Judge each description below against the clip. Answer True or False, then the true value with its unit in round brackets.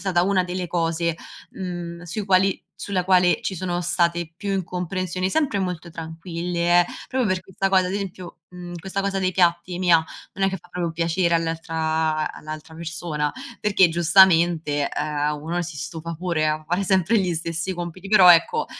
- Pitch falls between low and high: True (175 Hz)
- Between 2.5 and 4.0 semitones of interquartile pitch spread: False (2.1 semitones)